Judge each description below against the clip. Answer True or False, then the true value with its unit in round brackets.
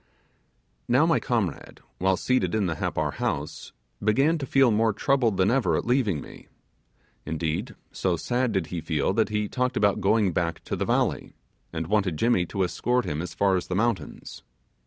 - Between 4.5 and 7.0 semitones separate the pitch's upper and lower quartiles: True (5.2 semitones)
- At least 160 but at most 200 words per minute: True (180 wpm)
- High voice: False (100 Hz)